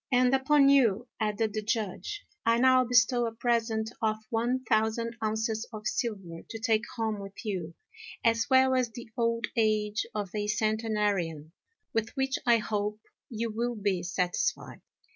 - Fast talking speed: No, average, 155 wpm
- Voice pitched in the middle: No, high, 225 Hz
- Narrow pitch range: Yes, narrow, 2.3 semitones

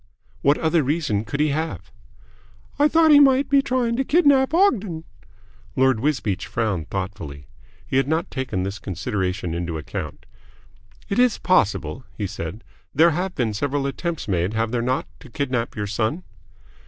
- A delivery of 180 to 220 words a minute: No, average, 160 wpm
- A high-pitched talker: No, low, 130 Hz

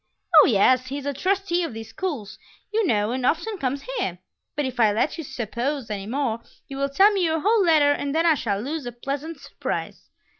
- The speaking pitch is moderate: No, very high, 280 Hz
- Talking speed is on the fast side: Yes, fast, 220 wpm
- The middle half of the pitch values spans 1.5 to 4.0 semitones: No, wide, 5.4 semitones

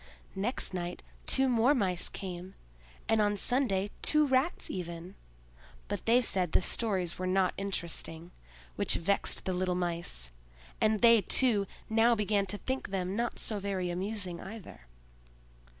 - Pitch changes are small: No, average, 3.9 semitones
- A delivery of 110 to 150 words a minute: Yes, average, 145 wpm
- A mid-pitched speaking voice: No, high, 195 Hz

